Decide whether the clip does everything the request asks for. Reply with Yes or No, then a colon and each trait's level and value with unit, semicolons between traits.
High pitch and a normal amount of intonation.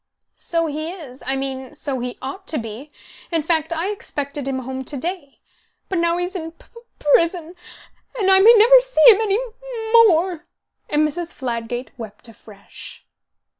No: very high, 325 Hz; wide, 6.2 semitones